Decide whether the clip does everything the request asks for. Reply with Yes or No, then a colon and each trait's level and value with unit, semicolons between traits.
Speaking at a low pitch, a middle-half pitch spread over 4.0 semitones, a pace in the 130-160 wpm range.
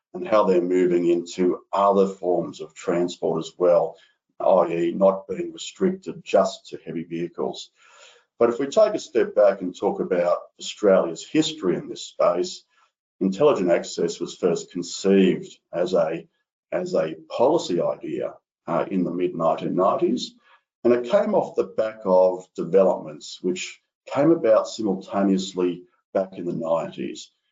Yes: very low, 95 Hz; average, 5.2 semitones; average, 145 wpm